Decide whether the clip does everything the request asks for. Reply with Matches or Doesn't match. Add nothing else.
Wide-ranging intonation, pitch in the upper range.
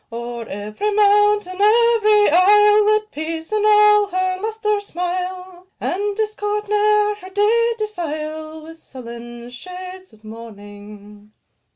Matches